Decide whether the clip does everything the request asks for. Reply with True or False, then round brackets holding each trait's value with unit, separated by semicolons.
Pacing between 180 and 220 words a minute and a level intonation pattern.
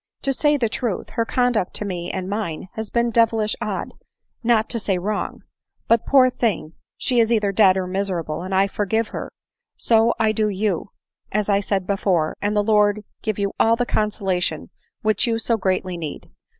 False (195 wpm; 3.1 semitones)